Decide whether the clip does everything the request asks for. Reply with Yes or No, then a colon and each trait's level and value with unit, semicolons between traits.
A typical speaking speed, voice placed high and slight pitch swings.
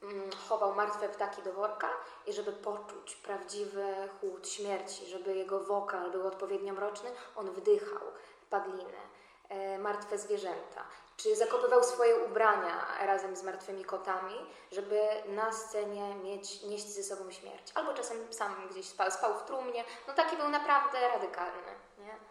Yes: average, 140 wpm; high, 205 Hz; narrow, 2.3 semitones